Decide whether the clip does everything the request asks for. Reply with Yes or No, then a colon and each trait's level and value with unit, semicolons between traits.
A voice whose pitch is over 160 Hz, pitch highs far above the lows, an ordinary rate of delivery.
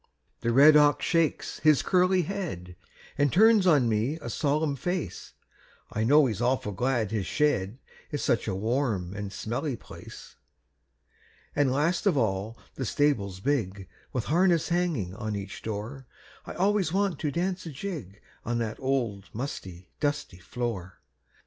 No: low, 130 Hz; wide, 6.6 semitones; average, 150 wpm